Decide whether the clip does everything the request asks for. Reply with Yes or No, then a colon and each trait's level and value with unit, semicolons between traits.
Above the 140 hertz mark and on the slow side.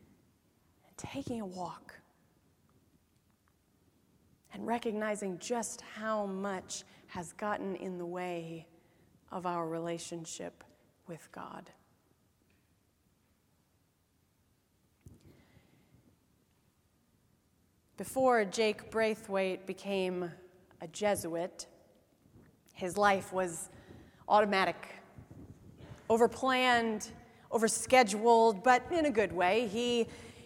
Yes: medium, 185 Hz; slow, 70 wpm